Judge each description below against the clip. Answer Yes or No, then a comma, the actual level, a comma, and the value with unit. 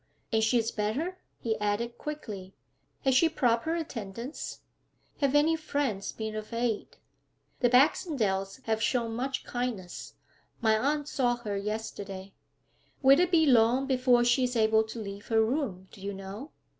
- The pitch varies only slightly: No, average, 4.2 semitones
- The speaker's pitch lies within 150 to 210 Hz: No, high, 235 Hz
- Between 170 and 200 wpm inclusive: No, average, 155 wpm